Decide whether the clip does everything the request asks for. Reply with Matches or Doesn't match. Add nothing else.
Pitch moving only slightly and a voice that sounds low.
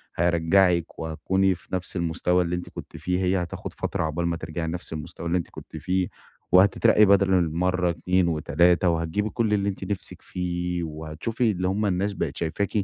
Matches